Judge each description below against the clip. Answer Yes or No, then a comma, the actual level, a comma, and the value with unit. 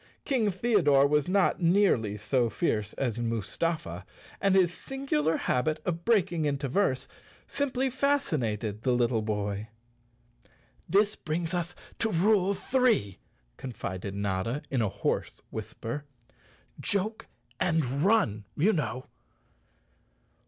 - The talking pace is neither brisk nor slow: No, slow, 115 wpm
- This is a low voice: No, medium, 155 Hz